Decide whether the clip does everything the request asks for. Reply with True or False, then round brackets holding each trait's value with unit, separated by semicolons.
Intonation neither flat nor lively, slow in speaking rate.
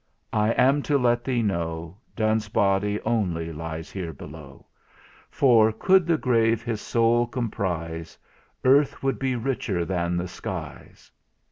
False (5.7 semitones; 130 wpm)